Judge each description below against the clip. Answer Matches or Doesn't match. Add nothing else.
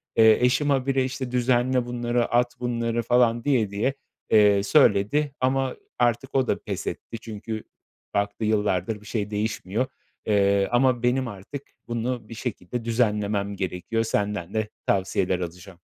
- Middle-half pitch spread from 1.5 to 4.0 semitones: Matches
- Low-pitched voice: Matches